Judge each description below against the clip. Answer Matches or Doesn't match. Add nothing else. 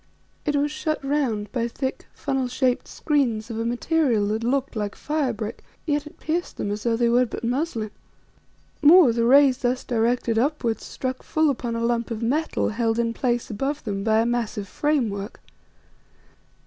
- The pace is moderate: Matches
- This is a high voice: Matches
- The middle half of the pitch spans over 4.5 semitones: Doesn't match